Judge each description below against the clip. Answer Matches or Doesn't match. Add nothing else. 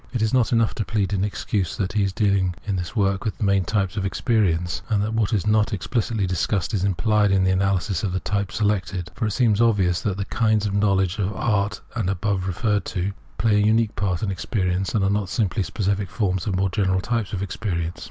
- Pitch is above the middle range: Doesn't match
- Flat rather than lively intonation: Matches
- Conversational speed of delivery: Doesn't match